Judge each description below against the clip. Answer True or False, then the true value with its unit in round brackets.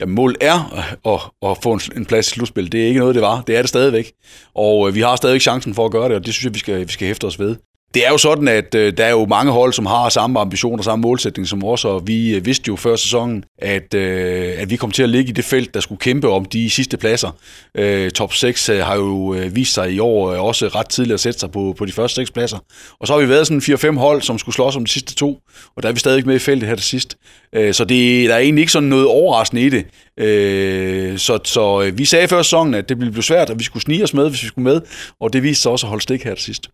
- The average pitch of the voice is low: True (115 Hz)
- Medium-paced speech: False (270 wpm)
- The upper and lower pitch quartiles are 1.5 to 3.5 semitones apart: False (4.0 semitones)